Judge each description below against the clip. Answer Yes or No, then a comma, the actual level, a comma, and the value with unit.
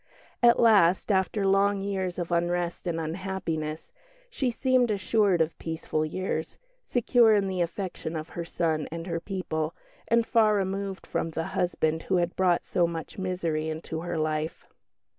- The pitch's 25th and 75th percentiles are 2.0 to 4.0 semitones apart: Yes, average, 3.3 semitones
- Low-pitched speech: No, medium, 180 Hz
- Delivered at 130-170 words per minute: Yes, average, 160 wpm